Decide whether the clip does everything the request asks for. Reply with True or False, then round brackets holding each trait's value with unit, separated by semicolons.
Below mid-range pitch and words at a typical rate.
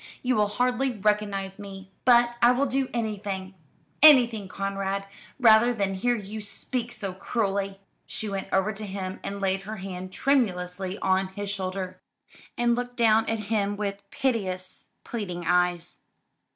False (200 Hz; 150 wpm)